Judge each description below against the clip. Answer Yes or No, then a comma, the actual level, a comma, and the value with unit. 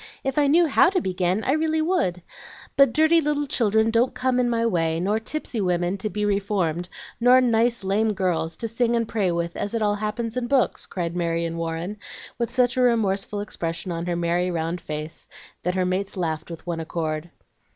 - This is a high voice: Yes, high, 205 Hz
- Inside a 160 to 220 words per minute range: Yes, average, 200 wpm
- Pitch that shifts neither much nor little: No, wide, 5.7 semitones